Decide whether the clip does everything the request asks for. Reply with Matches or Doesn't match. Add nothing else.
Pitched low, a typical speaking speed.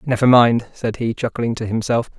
Matches